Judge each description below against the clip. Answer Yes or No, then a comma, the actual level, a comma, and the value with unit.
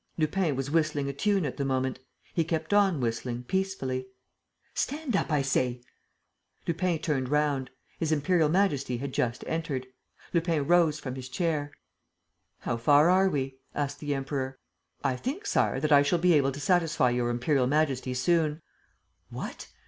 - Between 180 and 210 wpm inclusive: No, average, 160 wpm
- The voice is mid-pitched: Yes, medium, 145 Hz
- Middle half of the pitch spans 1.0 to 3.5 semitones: No, average, 4.1 semitones